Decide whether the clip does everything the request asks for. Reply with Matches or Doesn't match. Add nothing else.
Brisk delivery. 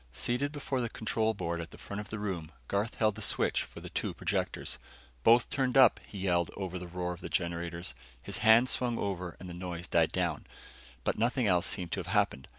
Matches